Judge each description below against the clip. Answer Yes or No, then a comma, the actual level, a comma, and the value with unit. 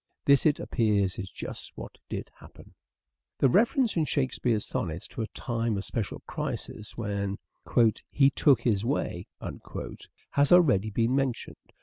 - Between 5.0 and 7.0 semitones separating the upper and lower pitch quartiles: Yes, wide, 5.5 semitones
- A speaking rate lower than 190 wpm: Yes, average, 140 wpm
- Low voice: Yes, low, 115 Hz